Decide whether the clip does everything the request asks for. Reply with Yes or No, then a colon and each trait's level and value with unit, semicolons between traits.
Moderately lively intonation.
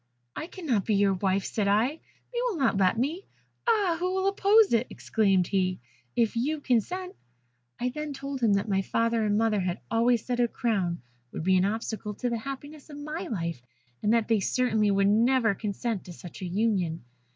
No: wide, 5.8 semitones